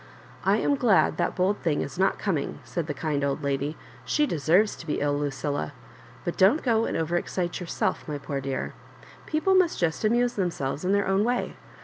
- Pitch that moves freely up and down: Yes, wide, 6.6 semitones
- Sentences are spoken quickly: Yes, fast, 210 wpm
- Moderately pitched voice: Yes, medium, 175 Hz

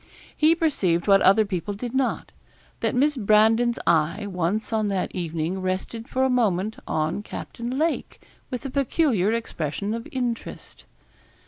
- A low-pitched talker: No, high, 215 Hz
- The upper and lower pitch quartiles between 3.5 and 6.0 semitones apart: Yes, average, 4.9 semitones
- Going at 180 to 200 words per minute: No, average, 145 wpm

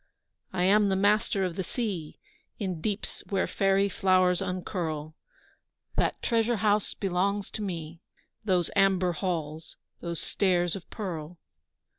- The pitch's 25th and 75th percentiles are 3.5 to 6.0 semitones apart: No, narrow, 2.5 semitones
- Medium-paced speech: No, slow, 130 wpm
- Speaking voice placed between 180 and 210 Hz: Yes, medium, 185 Hz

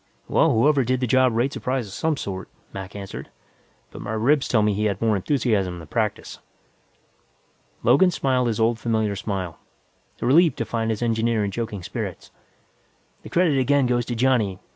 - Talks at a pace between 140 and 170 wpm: No, average, 180 wpm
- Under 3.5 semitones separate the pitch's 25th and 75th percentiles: No, average, 4.0 semitones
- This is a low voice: Yes, low, 115 Hz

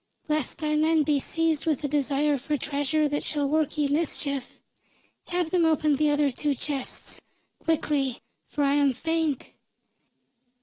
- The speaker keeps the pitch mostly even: Yes, narrow, 1.9 semitones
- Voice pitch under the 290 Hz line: No, very high, 295 Hz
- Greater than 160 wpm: No, average, 150 wpm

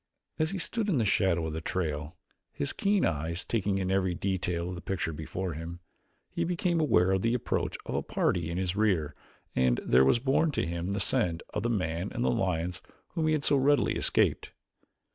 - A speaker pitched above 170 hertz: No, very low, 95 Hz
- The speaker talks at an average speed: No, fast, 210 wpm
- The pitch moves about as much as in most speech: No, wide, 6.1 semitones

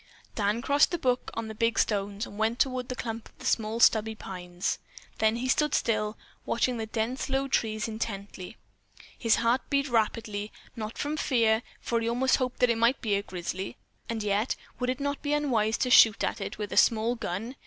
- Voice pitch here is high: Yes, high, 230 Hz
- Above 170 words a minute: Yes, average, 200 wpm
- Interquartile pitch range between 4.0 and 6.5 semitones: No, average, 2.8 semitones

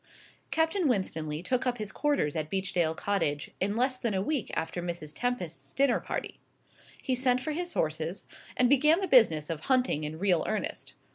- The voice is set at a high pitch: Yes, high, 205 Hz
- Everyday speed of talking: Yes, average, 180 wpm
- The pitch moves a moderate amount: No, wide, 8.0 semitones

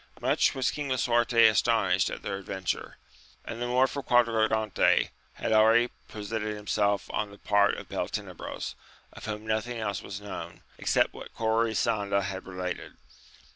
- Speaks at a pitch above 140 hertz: No, low, 110 Hz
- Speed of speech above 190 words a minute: No, average, 165 wpm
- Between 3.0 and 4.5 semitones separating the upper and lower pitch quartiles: No, narrow, 2.5 semitones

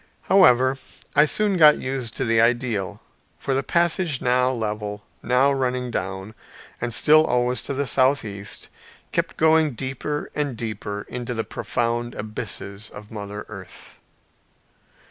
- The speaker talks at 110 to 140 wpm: Yes, slow, 135 wpm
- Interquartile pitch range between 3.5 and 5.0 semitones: Yes, average, 4.3 semitones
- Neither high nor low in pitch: No, low, 125 Hz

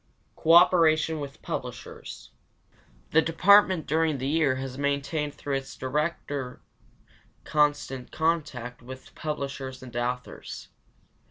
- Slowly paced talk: Yes, slow, 100 wpm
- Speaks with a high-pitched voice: No, medium, 145 Hz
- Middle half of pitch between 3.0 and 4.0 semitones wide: Yes, average, 3.4 semitones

